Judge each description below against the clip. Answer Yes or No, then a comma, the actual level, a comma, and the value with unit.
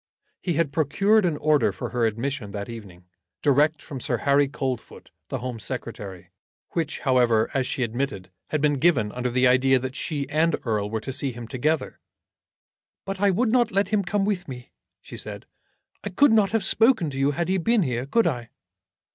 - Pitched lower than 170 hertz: Yes, medium, 140 Hz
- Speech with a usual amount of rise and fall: No, wide, 6.2 semitones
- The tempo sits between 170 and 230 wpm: Yes, average, 195 wpm